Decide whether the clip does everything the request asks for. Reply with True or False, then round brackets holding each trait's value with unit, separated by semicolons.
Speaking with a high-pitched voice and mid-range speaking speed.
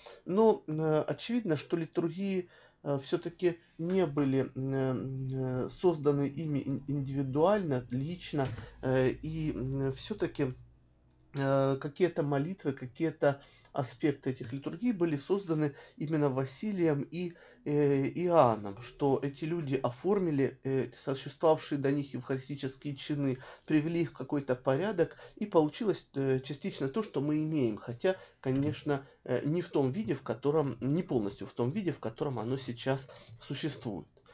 False (140 Hz; 125 wpm)